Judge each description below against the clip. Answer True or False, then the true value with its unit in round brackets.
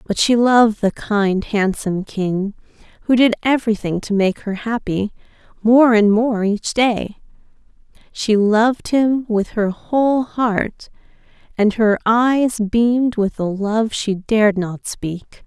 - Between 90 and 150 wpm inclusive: True (145 wpm)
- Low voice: False (220 Hz)